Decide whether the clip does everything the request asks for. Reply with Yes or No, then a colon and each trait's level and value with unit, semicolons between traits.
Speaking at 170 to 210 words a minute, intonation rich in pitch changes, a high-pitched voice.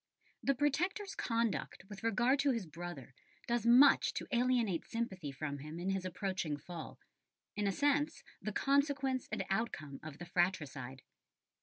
No: average, 150 wpm; wide, 7.4 semitones; high, 205 Hz